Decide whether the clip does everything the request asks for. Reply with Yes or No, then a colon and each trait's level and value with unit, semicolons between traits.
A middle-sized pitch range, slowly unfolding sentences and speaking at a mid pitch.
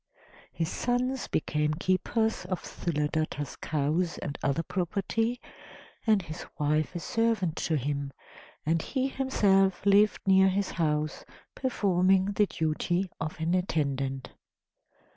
Yes: average, 4.7 semitones; slow, 120 wpm; medium, 180 Hz